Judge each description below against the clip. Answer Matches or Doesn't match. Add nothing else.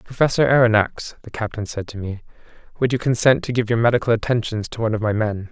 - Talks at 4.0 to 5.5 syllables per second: Doesn't match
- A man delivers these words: Matches